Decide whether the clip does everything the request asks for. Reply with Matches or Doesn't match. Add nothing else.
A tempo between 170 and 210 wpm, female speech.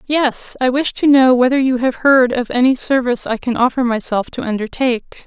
Matches